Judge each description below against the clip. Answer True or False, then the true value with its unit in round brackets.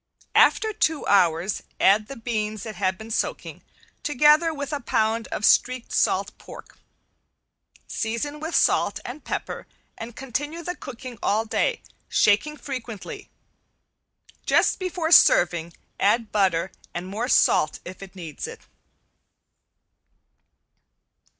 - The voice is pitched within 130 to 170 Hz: False (230 Hz)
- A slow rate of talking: True (120 wpm)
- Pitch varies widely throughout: True (6.5 semitones)